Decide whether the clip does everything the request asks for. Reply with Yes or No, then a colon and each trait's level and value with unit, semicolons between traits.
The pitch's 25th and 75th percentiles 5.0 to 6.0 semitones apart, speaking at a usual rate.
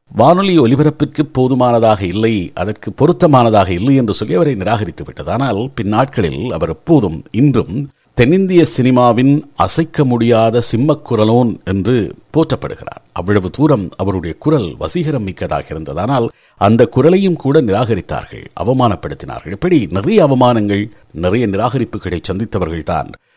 Yes: wide, 5.6 semitones; average, 110 wpm